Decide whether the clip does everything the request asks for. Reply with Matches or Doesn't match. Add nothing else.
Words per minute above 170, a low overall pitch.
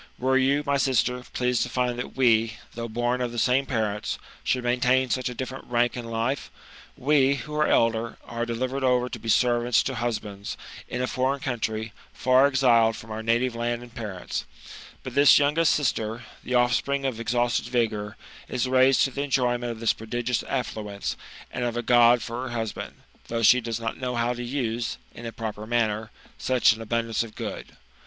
Matches